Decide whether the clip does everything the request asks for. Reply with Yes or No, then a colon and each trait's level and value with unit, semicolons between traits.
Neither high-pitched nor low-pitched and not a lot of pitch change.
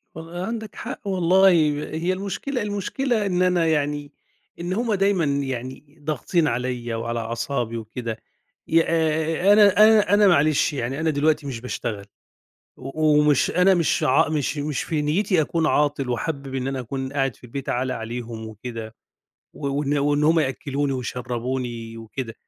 No: medium, 145 Hz; average, 5.2 semitones